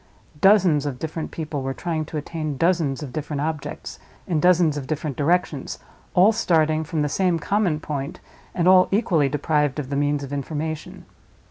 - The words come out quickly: No, average, 170 wpm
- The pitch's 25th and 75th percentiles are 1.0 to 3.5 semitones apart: Yes, average, 3.0 semitones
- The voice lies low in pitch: No, medium, 155 Hz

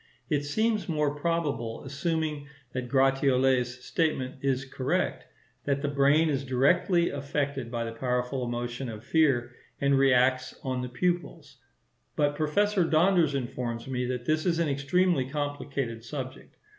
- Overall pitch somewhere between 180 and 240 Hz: No, medium, 140 Hz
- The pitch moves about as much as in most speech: Yes, average, 3.3 semitones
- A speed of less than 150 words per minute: Yes, average, 140 wpm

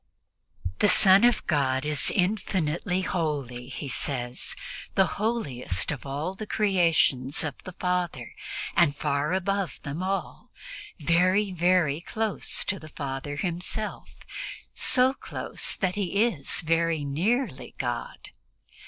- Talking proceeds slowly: Yes, slow, 120 wpm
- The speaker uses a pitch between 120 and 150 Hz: No, medium, 170 Hz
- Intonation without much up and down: No, average, 5.3 semitones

